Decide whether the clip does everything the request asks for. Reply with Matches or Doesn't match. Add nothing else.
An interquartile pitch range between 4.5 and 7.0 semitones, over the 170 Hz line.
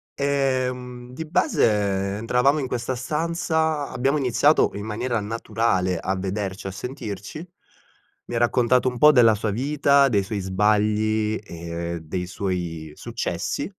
Doesn't match